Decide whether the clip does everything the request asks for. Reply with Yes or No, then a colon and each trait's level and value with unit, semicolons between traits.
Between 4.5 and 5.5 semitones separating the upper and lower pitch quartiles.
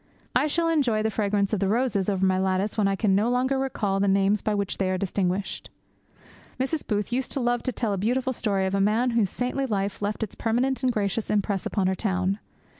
No: average, 3.9 semitones